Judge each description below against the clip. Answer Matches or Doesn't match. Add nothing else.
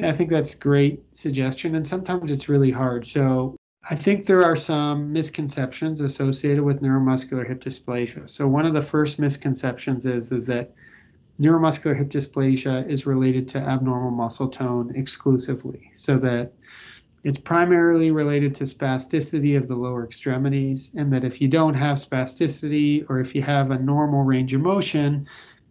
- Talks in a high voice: Doesn't match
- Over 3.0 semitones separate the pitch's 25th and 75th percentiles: Doesn't match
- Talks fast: Doesn't match